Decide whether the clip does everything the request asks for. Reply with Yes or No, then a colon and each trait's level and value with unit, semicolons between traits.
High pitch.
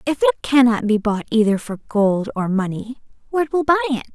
Yes: high, 245 Hz